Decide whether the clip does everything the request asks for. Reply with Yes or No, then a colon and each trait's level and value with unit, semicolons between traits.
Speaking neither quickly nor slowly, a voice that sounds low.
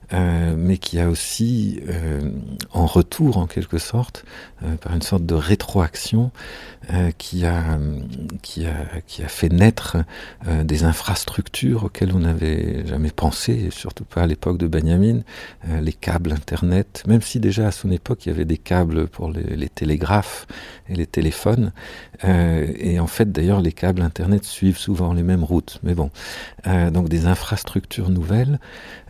Yes: average, 170 wpm; very low, 85 Hz